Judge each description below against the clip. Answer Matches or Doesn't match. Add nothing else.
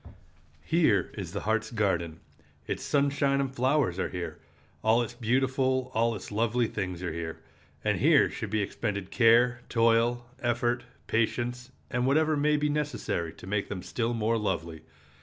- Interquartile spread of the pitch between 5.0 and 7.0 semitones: Doesn't match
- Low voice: Matches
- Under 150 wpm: Doesn't match